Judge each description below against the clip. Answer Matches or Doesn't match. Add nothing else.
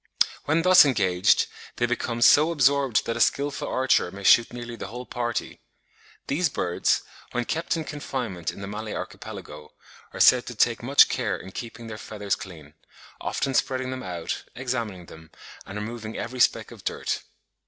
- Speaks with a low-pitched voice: Matches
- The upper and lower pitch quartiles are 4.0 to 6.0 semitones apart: Matches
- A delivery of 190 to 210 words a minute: Doesn't match